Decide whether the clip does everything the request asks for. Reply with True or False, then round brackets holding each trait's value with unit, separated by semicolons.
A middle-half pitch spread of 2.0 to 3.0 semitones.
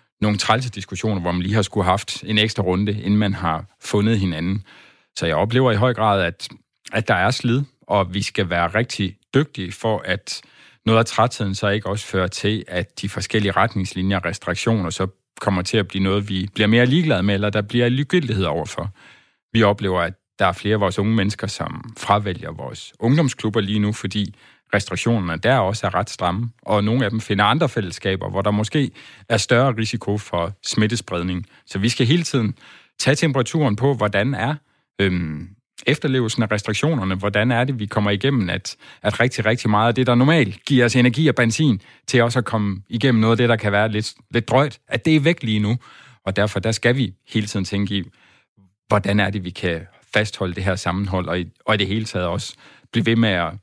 False (3.5 semitones)